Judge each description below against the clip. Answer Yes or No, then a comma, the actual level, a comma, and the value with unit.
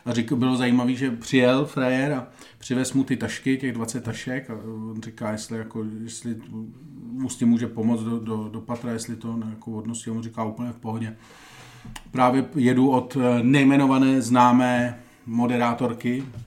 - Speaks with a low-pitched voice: Yes, low, 120 Hz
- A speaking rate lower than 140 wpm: No, fast, 170 wpm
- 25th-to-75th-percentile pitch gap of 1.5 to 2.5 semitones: Yes, narrow, 2.0 semitones